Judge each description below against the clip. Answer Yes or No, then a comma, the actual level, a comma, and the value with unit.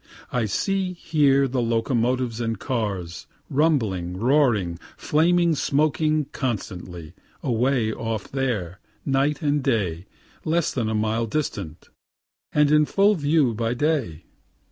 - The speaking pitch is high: No, low, 125 Hz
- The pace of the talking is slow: Yes, slow, 120 wpm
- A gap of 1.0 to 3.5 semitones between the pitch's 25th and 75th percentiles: No, wide, 5.5 semitones